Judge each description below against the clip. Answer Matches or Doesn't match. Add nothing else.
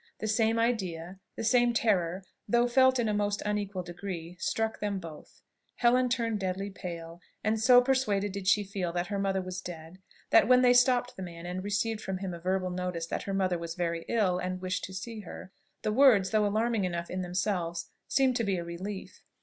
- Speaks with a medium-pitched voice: Doesn't match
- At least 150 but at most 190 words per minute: Doesn't match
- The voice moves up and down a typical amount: Matches